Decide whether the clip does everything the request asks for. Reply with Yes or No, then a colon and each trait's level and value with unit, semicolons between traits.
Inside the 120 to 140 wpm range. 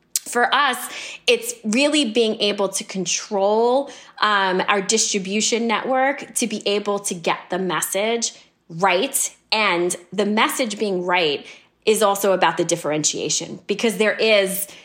Yes: slow, 135 wpm